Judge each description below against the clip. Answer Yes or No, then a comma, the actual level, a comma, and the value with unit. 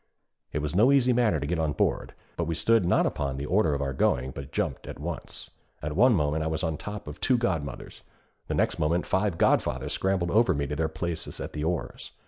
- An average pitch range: Yes, average, 4.7 semitones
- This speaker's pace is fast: Yes, fast, 230 wpm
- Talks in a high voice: No, very low, 80 Hz